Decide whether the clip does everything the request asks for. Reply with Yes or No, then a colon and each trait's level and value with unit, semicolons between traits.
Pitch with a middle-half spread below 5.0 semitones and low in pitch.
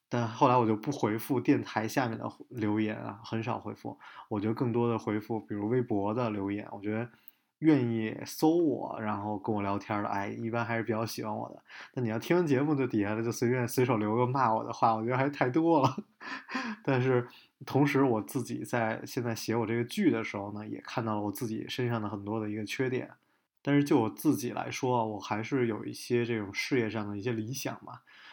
Yes: average, 3.1 semitones; low, 115 Hz